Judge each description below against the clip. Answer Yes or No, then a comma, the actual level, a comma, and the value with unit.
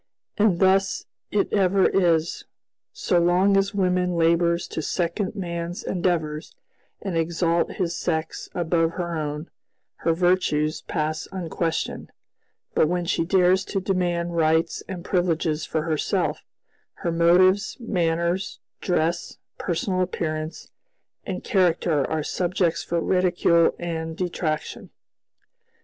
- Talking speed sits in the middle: No, slow, 115 wpm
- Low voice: No, medium, 170 Hz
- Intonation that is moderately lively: No, narrow, 2.0 semitones